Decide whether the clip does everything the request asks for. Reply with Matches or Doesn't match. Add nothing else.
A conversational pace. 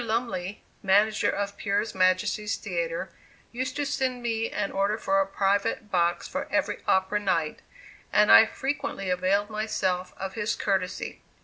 Matches